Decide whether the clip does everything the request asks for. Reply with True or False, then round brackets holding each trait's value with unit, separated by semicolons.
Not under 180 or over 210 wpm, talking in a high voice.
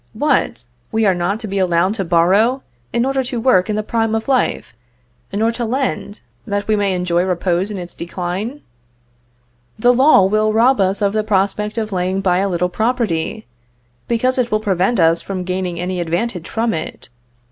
True (185 wpm; 200 Hz)